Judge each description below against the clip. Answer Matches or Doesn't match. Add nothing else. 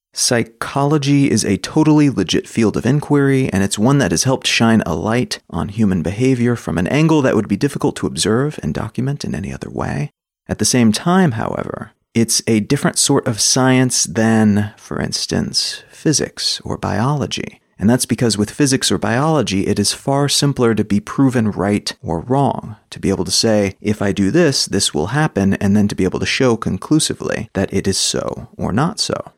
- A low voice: Matches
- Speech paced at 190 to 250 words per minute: Matches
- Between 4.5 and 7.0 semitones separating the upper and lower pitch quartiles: Matches